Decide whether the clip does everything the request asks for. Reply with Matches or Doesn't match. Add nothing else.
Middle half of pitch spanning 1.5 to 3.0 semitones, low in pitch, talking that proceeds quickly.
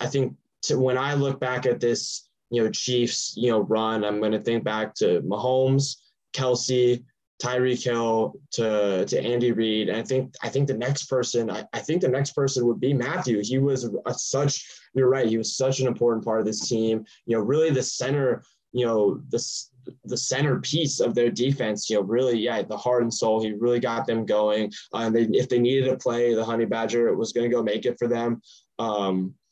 Matches